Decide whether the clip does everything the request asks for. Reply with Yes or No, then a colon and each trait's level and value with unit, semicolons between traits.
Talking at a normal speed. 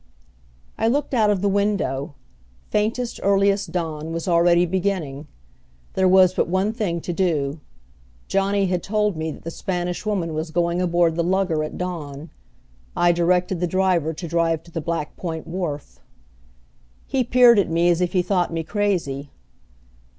Yes: average, 165 wpm